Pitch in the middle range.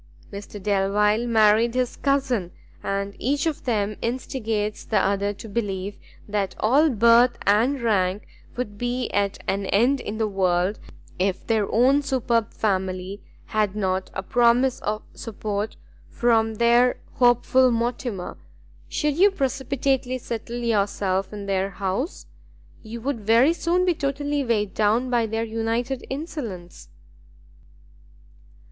No: high, 225 Hz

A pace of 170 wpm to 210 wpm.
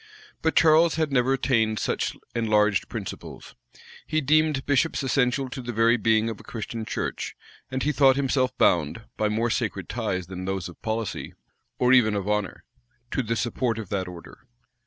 Yes: average, 175 wpm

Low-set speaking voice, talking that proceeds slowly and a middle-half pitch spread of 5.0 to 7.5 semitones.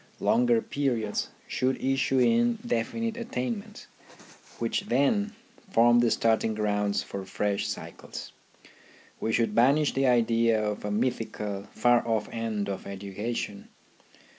No: low, 115 Hz; slow, 120 wpm; average, 4.2 semitones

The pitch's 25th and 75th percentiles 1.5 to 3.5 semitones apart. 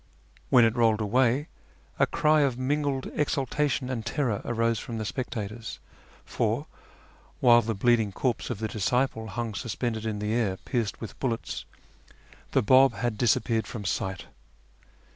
Yes: average, 2.9 semitones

